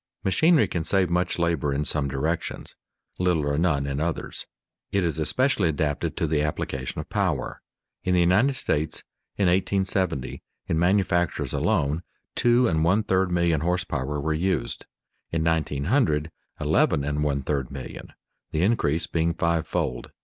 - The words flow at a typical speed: Yes, average, 155 wpm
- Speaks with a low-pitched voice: Yes, very low, 80 Hz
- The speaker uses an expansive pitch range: No, average, 3.7 semitones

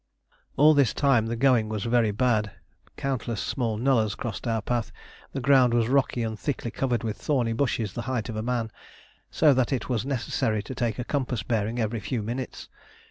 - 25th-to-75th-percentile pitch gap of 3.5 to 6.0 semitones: No, average, 2.8 semitones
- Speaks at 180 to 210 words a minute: Yes, average, 190 wpm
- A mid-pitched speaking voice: No, low, 120 Hz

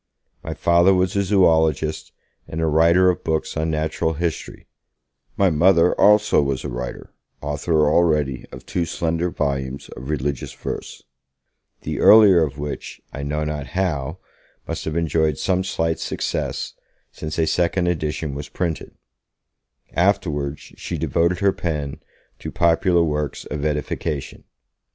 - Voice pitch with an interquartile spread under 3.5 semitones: Yes, average, 2.8 semitones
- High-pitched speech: No, very low, 80 Hz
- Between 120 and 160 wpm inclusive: Yes, average, 140 wpm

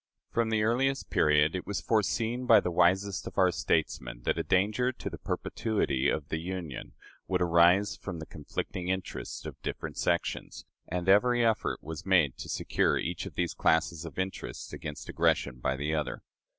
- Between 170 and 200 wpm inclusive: Yes, average, 175 wpm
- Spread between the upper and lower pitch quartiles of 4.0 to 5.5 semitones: Yes, average, 4.6 semitones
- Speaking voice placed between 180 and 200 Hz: No, very low, 90 Hz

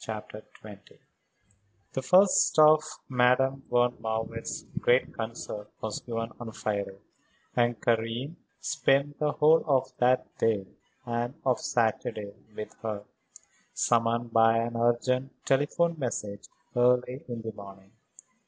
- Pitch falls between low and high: No, low, 120 Hz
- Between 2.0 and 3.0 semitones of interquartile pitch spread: Yes, average, 2.7 semitones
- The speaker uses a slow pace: Yes, slow, 120 wpm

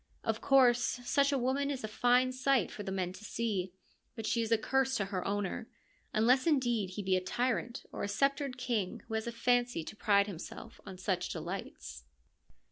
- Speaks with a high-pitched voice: Yes, high, 225 Hz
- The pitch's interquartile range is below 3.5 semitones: No, average, 4.4 semitones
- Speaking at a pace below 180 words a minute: No, average, 195 wpm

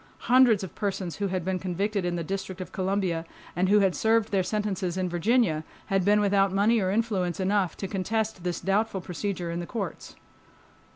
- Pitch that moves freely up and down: No, narrow, 2.4 semitones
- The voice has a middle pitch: No, high, 195 Hz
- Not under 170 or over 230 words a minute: Yes, average, 190 wpm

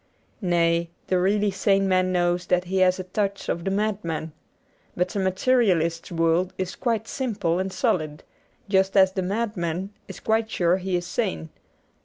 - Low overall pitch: No, medium, 185 Hz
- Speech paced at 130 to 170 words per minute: Yes, average, 165 wpm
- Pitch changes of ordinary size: No, narrow, 2.3 semitones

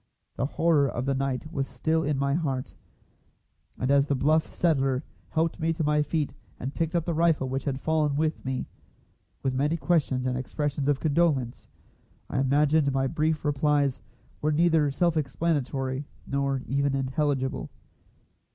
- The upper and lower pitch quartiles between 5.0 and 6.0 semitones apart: No, average, 2.8 semitones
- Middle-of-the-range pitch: Yes, medium, 145 Hz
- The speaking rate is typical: Yes, average, 160 wpm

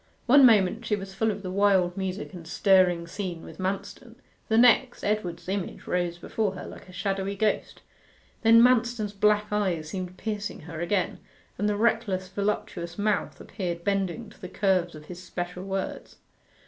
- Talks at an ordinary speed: Yes, average, 170 wpm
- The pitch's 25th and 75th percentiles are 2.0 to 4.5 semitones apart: Yes, average, 2.8 semitones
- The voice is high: Yes, high, 195 Hz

